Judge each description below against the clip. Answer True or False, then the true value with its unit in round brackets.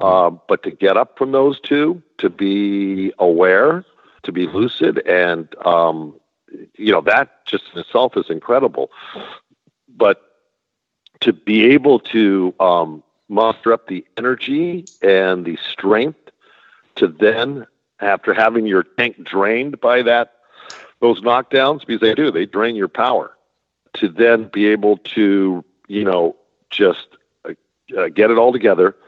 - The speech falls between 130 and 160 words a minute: True (140 wpm)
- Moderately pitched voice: False (105 Hz)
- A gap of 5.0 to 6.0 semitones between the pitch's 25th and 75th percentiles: False (4.2 semitones)